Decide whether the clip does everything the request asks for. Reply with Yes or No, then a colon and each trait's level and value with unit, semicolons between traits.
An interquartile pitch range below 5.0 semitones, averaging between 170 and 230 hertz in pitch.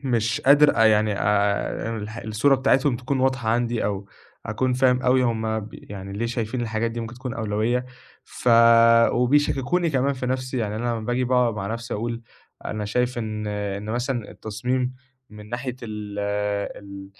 No: average, 3.0 semitones; low, 115 Hz